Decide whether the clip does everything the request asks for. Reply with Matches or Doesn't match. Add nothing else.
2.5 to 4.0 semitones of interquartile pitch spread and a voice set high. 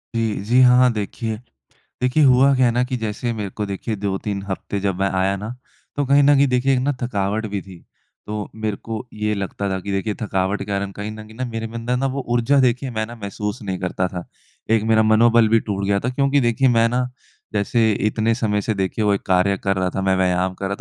Doesn't match